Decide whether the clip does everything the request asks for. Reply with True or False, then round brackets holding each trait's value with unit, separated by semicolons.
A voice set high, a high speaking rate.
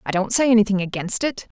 True (215 Hz; 225 wpm)